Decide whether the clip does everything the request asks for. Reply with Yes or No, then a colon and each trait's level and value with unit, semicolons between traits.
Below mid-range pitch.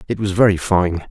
Yes: very low, 95 Hz